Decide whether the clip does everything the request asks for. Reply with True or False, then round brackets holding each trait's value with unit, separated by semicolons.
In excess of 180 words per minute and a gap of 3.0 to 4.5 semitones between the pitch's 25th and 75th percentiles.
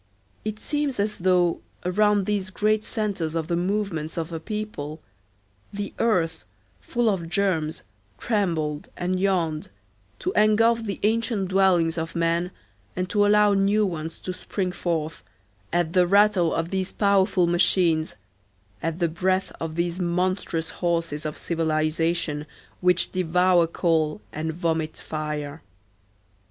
False (135 wpm; 3.5 semitones)